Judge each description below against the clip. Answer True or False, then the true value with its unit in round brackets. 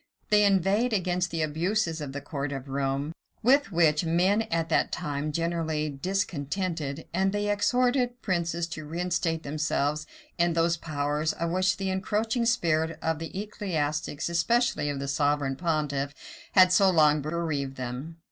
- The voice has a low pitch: False (165 Hz)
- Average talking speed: True (155 wpm)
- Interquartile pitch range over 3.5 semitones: True (4.2 semitones)